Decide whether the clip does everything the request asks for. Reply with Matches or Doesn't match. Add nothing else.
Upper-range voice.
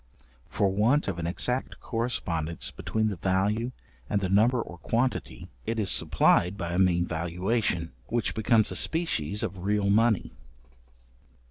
Doesn't match